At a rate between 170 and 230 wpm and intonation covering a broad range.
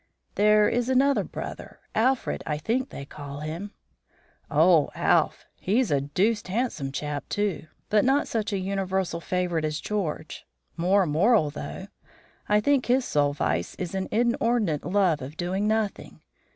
No: average, 150 wpm; wide, 6.1 semitones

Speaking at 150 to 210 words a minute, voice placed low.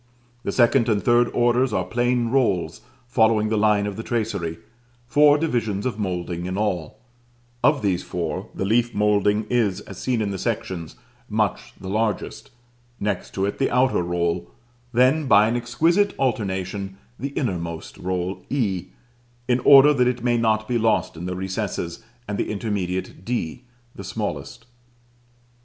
Yes: average, 155 wpm; low, 110 Hz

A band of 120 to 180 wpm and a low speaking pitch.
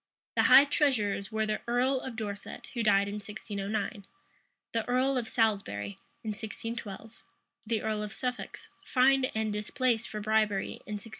No: average, 155 wpm; high, 220 Hz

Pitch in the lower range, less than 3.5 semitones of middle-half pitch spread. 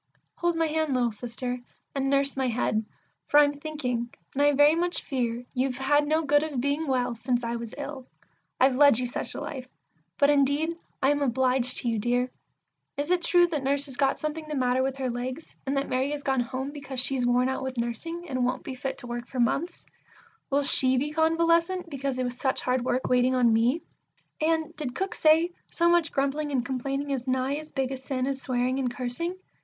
No: very high, 270 Hz; average, 2.8 semitones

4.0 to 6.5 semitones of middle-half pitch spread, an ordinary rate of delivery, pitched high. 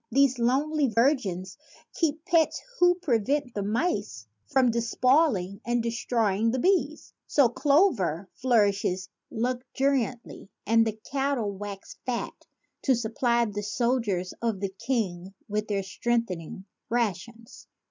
No: average, 4.6 semitones; slow, 115 wpm; high, 235 Hz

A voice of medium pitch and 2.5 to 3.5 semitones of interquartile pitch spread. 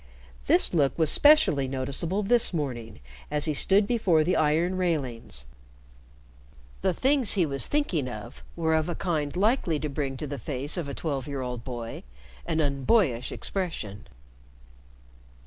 No: medium, 150 Hz; average, 5.2 semitones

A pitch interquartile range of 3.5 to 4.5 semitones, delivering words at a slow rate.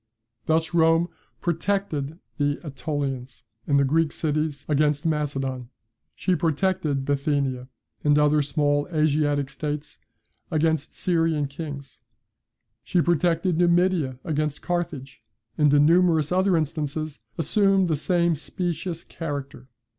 No: average, 2.8 semitones; slow, 115 wpm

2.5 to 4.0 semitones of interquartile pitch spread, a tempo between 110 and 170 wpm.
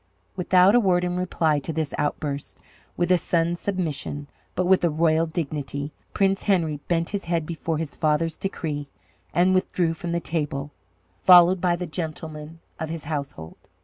Yes: average, 2.8 semitones; average, 165 wpm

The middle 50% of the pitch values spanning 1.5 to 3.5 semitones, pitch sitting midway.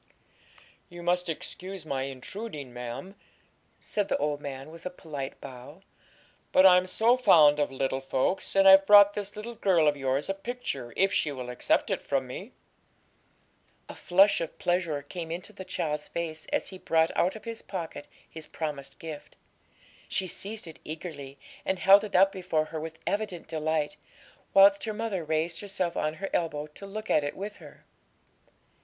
No: average, 4.7 semitones; medium, 170 Hz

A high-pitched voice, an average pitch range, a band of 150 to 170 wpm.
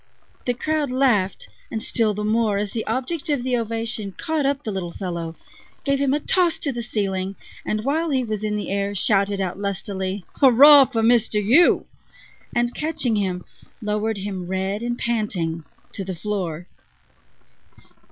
Yes: high, 215 Hz; average, 4.6 semitones; average, 165 wpm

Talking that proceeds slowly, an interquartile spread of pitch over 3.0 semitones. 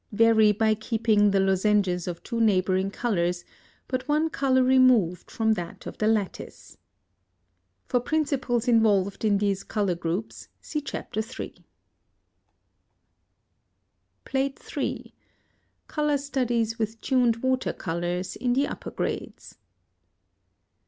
Yes: slow, 115 wpm; average, 4.7 semitones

